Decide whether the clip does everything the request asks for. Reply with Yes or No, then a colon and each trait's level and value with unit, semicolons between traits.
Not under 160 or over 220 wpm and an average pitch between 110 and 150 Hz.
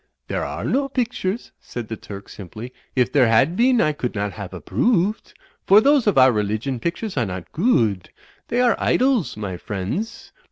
Yes: average, 190 wpm; low, 135 Hz